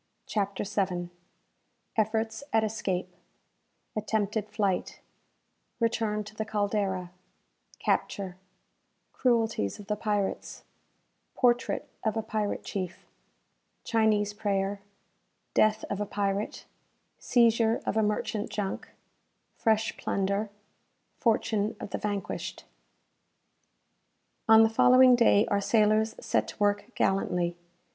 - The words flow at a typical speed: No, slow, 105 wpm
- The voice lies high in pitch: Yes, high, 210 Hz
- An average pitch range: No, narrow, 1.8 semitones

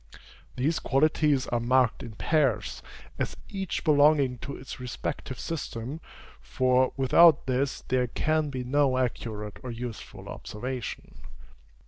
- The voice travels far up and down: No, average, 3.0 semitones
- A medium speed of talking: No, slow, 120 wpm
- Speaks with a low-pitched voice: Yes, low, 130 Hz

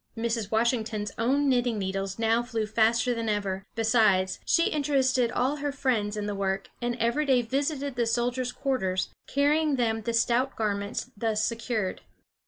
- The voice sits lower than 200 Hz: No, high, 230 Hz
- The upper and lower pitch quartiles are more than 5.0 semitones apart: No, average, 3.3 semitones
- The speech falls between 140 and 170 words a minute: Yes, average, 160 wpm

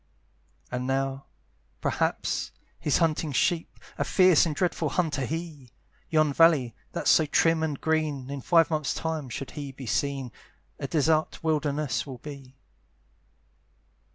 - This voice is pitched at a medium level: Yes, medium, 150 Hz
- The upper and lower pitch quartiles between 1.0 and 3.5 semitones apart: Yes, average, 2.9 semitones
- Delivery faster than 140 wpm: No, slow, 135 wpm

